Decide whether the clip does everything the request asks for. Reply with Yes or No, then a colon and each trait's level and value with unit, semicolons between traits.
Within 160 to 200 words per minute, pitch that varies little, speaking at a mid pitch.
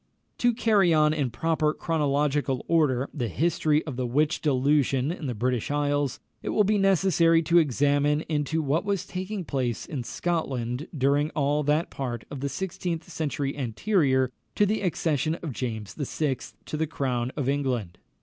No: average, 165 wpm; average, 3.8 semitones; medium, 145 Hz